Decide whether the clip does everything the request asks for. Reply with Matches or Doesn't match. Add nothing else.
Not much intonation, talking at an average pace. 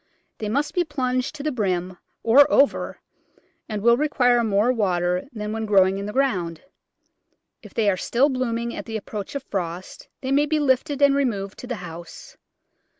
Doesn't match